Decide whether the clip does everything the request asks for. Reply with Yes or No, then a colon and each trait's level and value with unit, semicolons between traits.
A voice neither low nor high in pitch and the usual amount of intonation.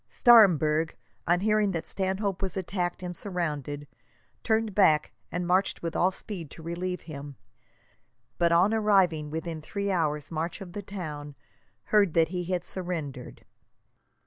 Yes: medium, 175 Hz; average, 3.4 semitones